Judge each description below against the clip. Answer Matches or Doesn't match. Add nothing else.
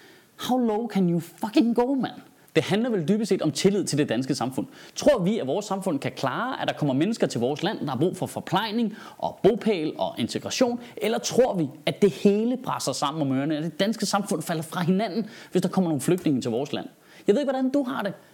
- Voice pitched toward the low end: Doesn't match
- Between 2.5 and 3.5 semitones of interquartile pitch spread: Doesn't match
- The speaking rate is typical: Doesn't match